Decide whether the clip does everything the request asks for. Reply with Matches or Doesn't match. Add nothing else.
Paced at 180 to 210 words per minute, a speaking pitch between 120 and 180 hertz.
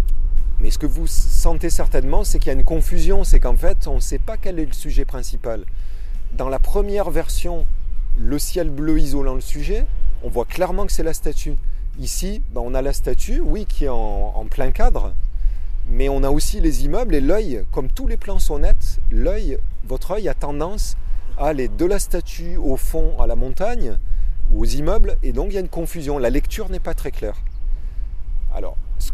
Matches